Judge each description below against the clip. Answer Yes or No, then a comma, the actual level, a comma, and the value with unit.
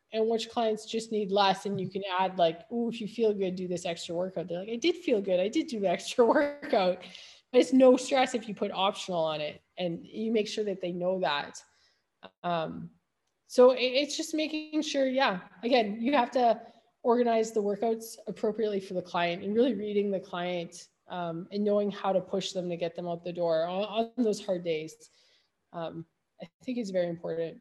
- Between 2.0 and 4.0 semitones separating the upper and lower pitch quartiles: No, average, 4.7 semitones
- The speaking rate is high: Yes, fast, 210 wpm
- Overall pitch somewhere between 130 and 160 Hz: No, high, 205 Hz